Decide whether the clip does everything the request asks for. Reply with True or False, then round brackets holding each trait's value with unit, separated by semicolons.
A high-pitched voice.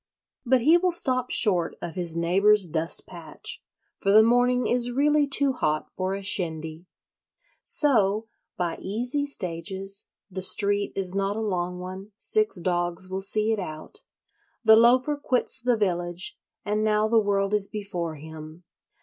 True (200 Hz)